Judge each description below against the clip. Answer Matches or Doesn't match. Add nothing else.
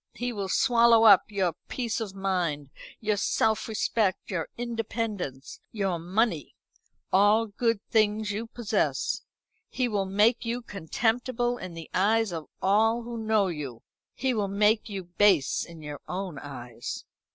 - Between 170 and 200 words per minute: Doesn't match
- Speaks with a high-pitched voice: Matches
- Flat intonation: Doesn't match